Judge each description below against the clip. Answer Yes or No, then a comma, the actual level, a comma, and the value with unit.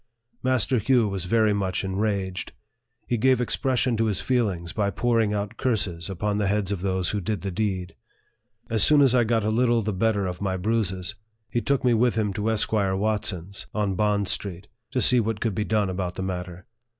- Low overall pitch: Yes, low, 105 Hz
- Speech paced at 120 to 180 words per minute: No, average, 200 wpm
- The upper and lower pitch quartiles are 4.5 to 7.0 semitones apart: No, average, 3.0 semitones